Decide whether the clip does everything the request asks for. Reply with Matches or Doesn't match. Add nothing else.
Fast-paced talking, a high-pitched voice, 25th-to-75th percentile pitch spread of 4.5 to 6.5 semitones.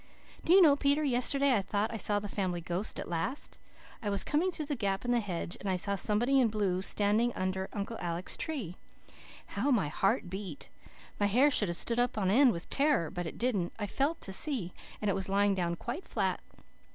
Matches